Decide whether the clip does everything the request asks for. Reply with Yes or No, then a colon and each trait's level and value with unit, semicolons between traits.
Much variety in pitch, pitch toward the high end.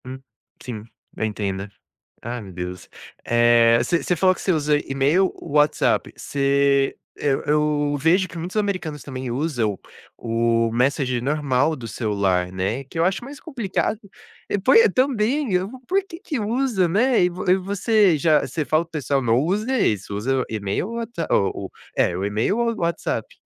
No: wide, 8.3 semitones; medium, 150 Hz